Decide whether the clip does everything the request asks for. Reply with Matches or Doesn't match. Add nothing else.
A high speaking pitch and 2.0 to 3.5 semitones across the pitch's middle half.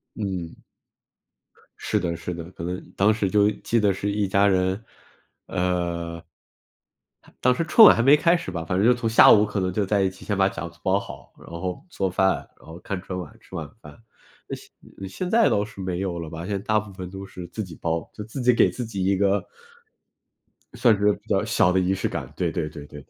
Doesn't match